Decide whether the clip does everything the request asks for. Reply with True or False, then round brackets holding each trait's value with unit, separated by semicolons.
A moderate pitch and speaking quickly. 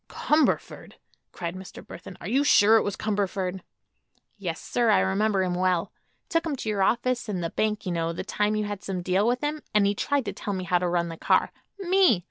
False (200 Hz; 225 wpm)